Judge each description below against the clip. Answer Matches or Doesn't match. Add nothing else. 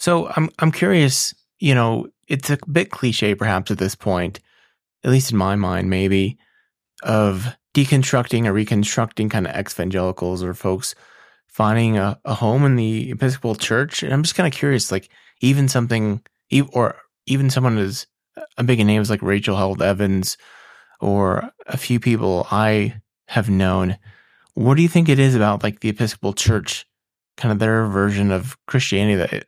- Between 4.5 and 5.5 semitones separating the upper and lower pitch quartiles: Matches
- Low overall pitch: Matches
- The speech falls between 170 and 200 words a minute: Matches